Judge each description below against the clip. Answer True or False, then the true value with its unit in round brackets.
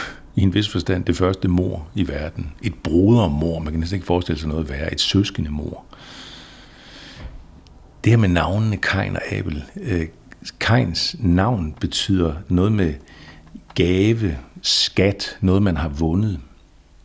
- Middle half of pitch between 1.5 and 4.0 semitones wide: True (3.7 semitones)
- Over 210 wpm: False (145 wpm)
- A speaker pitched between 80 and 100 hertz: True (90 Hz)